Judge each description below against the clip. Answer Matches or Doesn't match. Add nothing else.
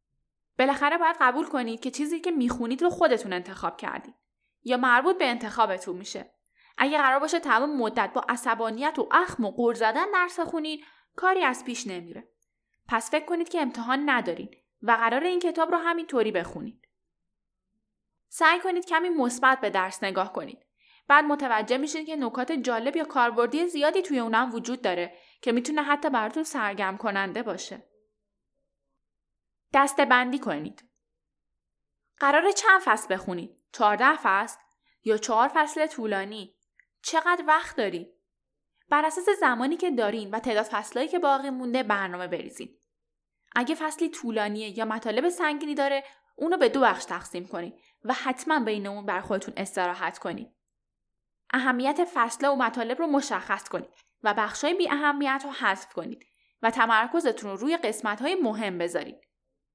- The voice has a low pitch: Doesn't match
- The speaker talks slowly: Doesn't match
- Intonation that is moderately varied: Doesn't match